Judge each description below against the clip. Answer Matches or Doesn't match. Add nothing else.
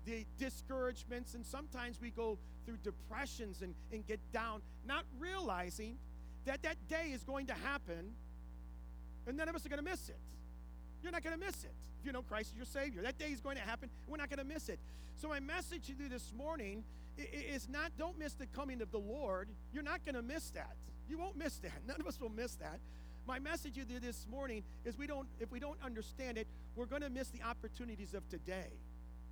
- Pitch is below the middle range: Doesn't match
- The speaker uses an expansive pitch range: Matches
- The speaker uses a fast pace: Matches